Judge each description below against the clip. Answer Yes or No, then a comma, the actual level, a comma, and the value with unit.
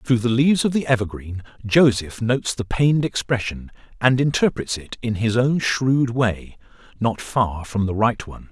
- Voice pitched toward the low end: Yes, low, 115 Hz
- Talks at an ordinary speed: Yes, average, 170 wpm